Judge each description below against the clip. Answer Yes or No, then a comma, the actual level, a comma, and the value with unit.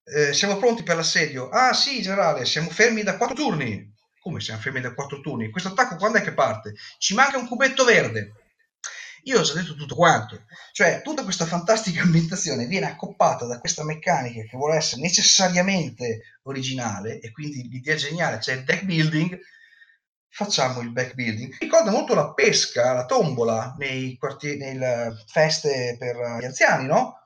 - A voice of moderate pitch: Yes, medium, 155 Hz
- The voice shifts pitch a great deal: Yes, wide, 7.5 semitones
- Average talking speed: No, fast, 175 wpm